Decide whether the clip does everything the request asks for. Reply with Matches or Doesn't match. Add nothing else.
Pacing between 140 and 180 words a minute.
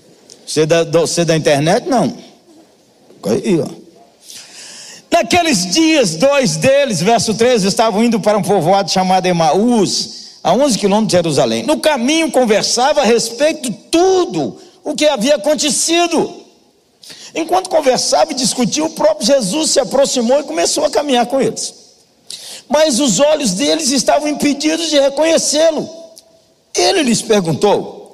Doesn't match